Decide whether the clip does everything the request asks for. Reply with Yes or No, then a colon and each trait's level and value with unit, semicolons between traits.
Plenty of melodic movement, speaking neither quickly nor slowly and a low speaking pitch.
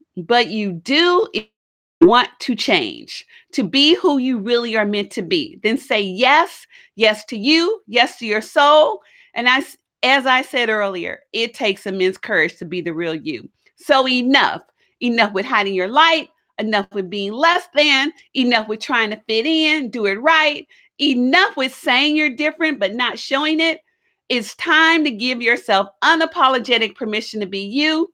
No: wide, 6.4 semitones; average, 170 wpm; very high, 255 Hz